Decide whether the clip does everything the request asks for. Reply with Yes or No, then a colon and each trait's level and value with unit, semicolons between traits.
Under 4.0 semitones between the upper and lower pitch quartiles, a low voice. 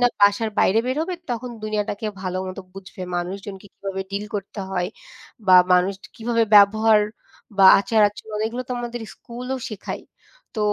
No: average, 3.0 semitones; high, 210 Hz